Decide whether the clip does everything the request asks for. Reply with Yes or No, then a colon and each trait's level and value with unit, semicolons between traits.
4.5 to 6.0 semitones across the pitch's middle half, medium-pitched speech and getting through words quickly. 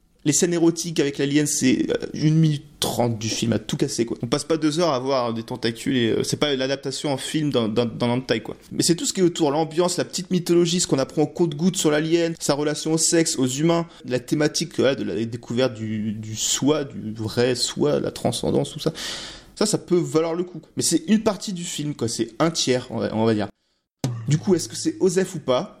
Yes: average, 5.2 semitones; medium, 150 Hz; fast, 250 wpm